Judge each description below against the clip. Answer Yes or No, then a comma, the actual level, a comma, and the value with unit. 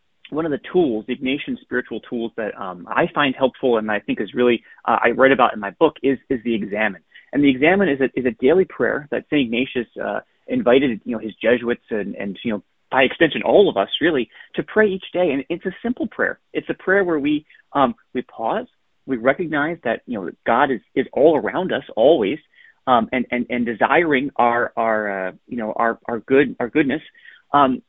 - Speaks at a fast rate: Yes, fast, 220 wpm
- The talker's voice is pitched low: Yes, low, 130 Hz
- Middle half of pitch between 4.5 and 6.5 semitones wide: No, average, 3.8 semitones